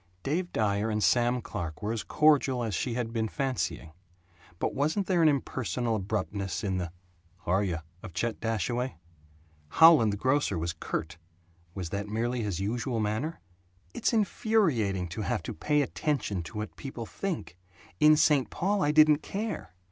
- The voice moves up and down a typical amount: No, wide, 6.6 semitones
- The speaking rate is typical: Yes, average, 165 wpm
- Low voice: Yes, low, 115 Hz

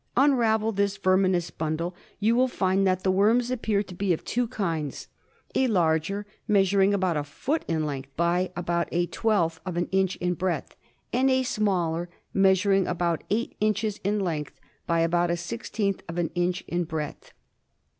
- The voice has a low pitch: No, medium, 185 Hz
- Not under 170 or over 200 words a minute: Yes, average, 175 wpm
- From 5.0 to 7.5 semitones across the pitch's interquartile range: No, average, 3.4 semitones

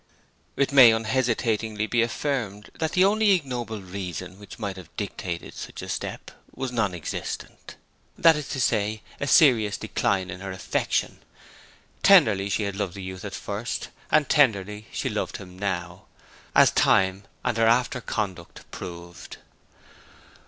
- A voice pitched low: Yes, low, 105 Hz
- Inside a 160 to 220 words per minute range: No, average, 150 wpm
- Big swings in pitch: No, average, 4.5 semitones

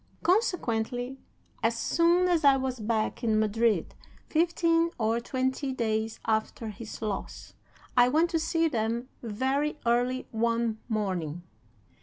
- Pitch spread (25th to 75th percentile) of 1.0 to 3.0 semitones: No, average, 4.8 semitones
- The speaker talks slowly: Yes, slow, 125 wpm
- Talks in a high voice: Yes, high, 240 Hz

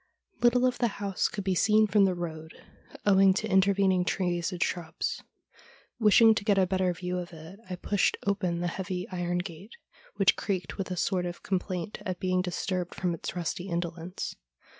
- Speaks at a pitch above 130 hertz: Yes, medium, 185 Hz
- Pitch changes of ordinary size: No, narrow, 2.1 semitones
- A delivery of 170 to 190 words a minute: Yes, average, 185 wpm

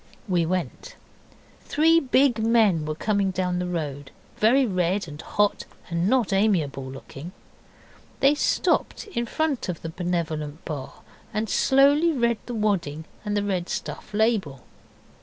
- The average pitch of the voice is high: Yes, high, 195 Hz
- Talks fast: No, average, 140 wpm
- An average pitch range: No, wide, 6.3 semitones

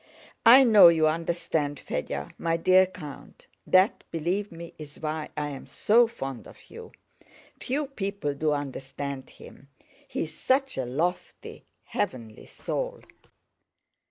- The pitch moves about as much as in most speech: No, wide, 5.7 semitones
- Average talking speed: No, slow, 130 wpm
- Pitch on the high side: No, medium, 165 Hz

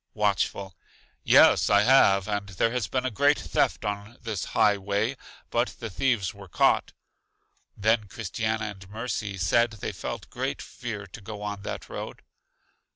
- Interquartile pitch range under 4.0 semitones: Yes, narrow, 2.5 semitones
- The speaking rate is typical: Yes, average, 155 wpm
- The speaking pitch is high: No, low, 105 Hz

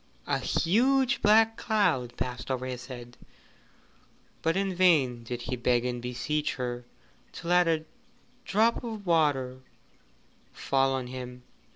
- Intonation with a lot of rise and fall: Yes, wide, 6.9 semitones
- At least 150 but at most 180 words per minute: No, slow, 135 wpm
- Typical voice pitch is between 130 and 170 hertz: Yes, low, 135 Hz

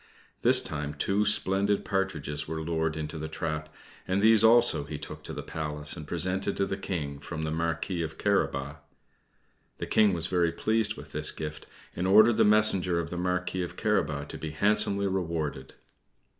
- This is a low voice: Yes, very low, 85 Hz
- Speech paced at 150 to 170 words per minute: No, average, 180 wpm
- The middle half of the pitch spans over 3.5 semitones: Yes, average, 4.1 semitones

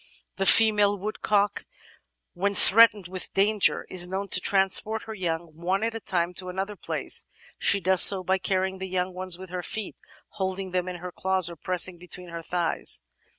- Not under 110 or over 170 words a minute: No, average, 185 wpm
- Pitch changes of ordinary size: No, narrow, 1.8 semitones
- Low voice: No, high, 190 Hz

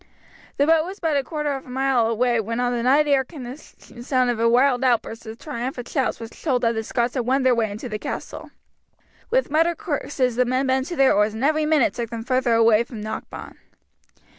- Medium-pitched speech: No, very high, 250 Hz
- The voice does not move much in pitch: No, average, 3.3 semitones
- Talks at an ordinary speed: No, fast, 230 wpm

